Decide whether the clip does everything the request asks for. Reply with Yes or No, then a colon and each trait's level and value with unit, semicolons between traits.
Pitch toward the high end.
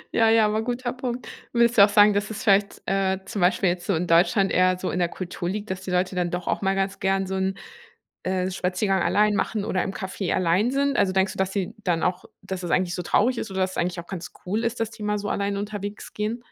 Yes: high, 195 Hz